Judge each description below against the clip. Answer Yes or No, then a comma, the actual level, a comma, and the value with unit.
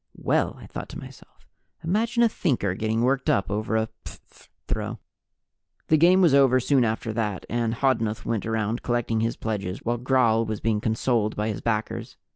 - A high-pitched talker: No, low, 115 Hz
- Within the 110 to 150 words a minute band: No, average, 180 wpm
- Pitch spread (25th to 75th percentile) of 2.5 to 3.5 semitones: Yes, average, 3.1 semitones